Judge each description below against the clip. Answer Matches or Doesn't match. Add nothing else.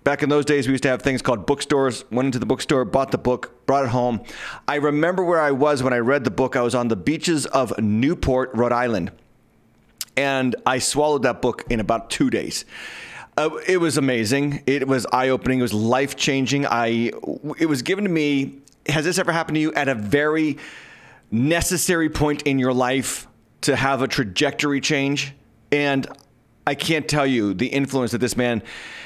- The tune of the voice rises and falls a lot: Doesn't match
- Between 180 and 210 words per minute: Matches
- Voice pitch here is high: Doesn't match